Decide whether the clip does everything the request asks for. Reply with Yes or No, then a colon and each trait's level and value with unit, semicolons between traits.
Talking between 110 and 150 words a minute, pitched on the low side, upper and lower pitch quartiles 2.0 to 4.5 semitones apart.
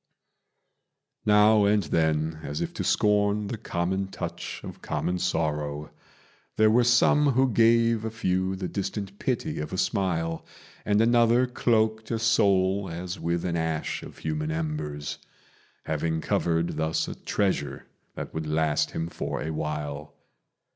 No: average, 145 wpm; very low, 95 Hz; wide, 5.4 semitones